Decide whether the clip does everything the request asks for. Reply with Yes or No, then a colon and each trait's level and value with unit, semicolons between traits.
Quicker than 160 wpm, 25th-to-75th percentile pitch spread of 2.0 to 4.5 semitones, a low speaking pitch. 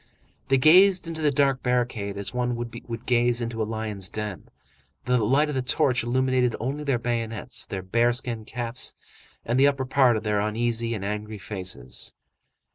Yes: average, 175 wpm; average, 3.1 semitones; low, 120 Hz